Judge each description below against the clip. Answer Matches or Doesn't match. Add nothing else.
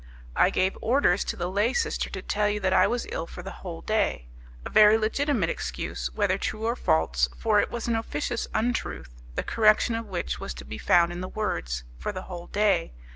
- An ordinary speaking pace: Doesn't match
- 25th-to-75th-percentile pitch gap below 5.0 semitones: Doesn't match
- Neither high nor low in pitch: Doesn't match